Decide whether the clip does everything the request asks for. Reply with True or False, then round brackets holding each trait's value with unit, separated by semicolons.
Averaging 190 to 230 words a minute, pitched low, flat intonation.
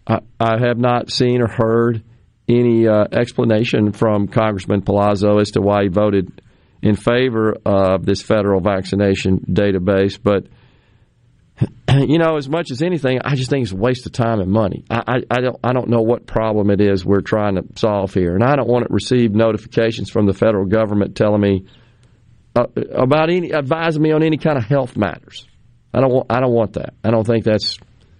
False (195 wpm; 115 Hz; 3.3 semitones)